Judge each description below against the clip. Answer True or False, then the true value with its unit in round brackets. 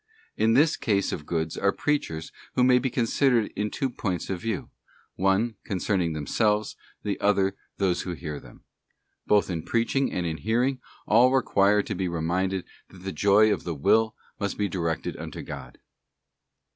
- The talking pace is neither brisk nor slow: True (170 wpm)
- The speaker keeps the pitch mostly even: False (4.2 semitones)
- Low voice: True (100 Hz)